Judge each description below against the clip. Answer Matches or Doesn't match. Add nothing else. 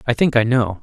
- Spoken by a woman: Doesn't match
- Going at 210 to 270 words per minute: Doesn't match